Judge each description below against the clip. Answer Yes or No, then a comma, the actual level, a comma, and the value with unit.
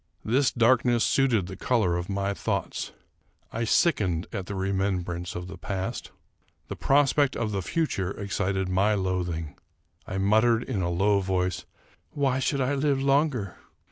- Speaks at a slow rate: No, average, 160 wpm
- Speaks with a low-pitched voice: Yes, low, 100 Hz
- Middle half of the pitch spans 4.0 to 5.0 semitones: No, wide, 5.4 semitones